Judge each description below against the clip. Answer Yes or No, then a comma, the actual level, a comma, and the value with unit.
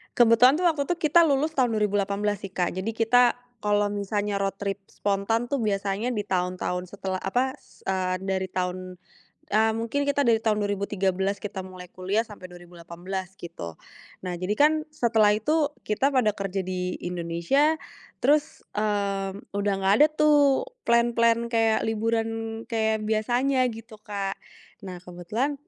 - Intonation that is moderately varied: Yes, average, 3.6 semitones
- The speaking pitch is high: Yes, high, 210 Hz